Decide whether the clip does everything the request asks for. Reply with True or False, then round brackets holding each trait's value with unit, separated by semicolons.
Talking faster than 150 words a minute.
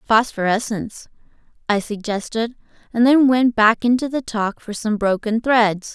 False (140 wpm)